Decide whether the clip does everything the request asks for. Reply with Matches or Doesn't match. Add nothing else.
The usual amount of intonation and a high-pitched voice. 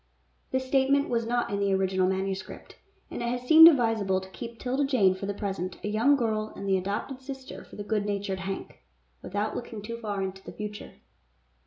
Matches